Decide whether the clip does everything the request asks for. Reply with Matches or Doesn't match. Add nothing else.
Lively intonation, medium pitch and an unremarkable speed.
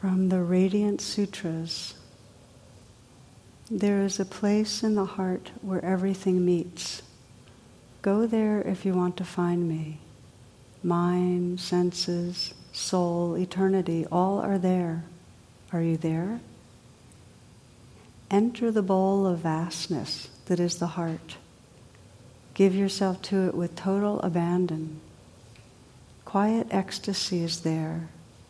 Doesn't match